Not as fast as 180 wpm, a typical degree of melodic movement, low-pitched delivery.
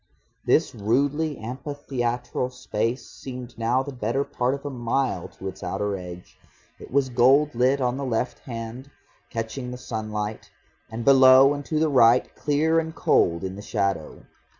Yes: average, 160 wpm; average, 3.5 semitones; low, 125 Hz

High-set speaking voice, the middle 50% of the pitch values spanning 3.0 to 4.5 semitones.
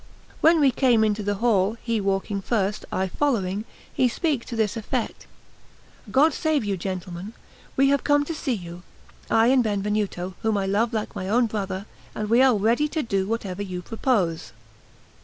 Yes: high, 215 Hz; average, 4.2 semitones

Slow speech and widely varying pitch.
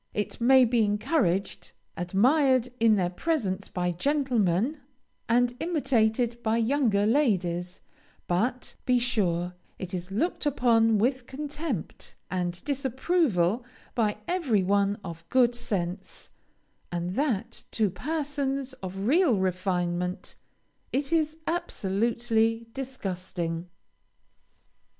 Yes: slow, 105 wpm; wide, 6.1 semitones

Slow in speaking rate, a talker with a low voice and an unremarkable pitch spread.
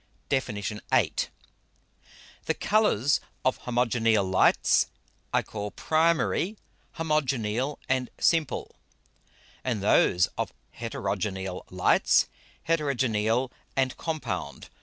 No: slow, 85 wpm; low, 125 Hz; wide, 5.9 semitones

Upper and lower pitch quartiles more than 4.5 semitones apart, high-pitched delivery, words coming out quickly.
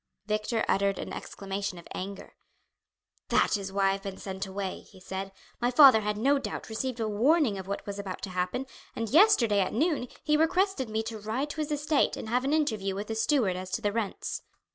Yes: wide, 5.4 semitones; high, 215 Hz; fast, 215 wpm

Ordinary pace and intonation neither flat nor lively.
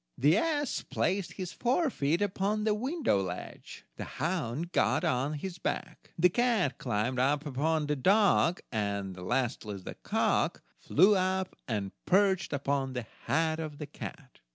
No: average, 150 wpm; wide, 6.9 semitones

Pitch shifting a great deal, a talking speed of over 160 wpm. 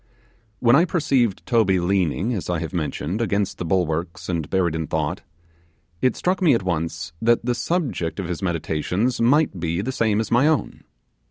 Yes: wide, 6.2 semitones; average, 180 wpm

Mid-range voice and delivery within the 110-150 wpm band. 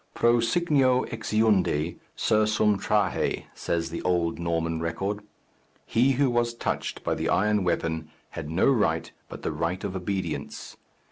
No: low, 100 Hz; average, 140 wpm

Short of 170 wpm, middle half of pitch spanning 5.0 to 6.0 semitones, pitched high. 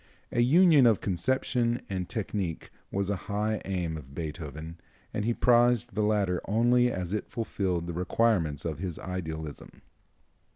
No: average, 150 wpm; wide, 5.5 semitones; low, 100 Hz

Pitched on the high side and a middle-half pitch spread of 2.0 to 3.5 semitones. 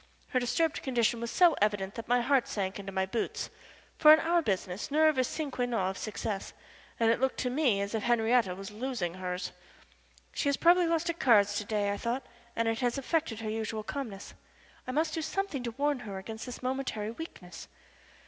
No: high, 235 Hz; average, 5.3 semitones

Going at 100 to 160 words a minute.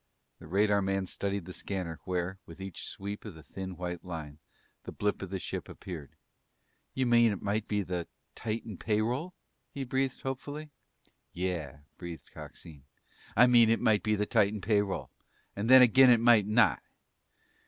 No: average, 170 wpm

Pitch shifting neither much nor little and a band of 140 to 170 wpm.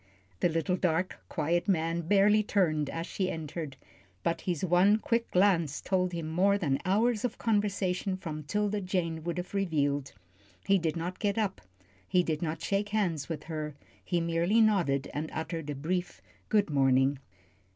Yes: average, 3.8 semitones; average, 165 wpm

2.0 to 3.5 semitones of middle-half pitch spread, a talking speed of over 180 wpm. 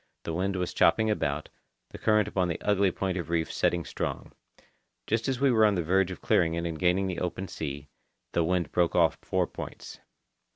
Yes: average, 2.8 semitones; average, 200 wpm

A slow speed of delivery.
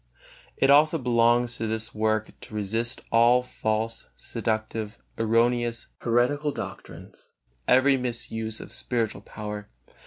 Yes: slow, 115 wpm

